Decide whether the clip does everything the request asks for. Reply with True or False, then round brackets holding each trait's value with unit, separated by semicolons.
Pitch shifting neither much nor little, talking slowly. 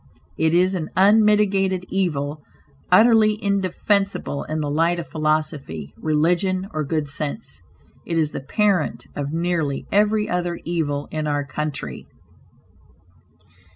True (4.3 semitones; 120 wpm)